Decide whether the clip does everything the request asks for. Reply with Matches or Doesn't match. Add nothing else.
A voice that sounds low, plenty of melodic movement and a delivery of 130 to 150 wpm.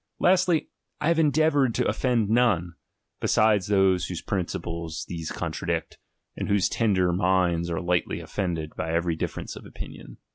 Matches